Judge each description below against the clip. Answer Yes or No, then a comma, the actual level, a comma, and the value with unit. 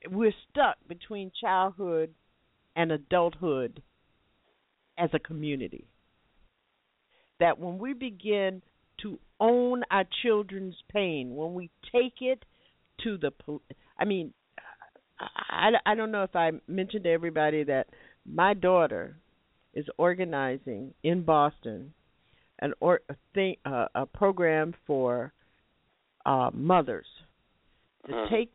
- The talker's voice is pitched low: No, medium, 175 Hz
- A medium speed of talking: No, slow, 115 wpm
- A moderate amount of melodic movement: Yes, average, 4.4 semitones